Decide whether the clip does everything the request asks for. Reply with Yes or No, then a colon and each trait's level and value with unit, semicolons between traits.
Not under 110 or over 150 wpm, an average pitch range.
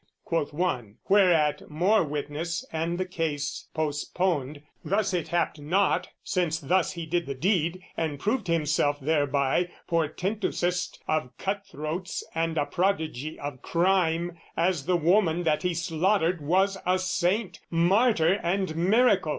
Yes: slow, 135 wpm; average, 3.3 semitones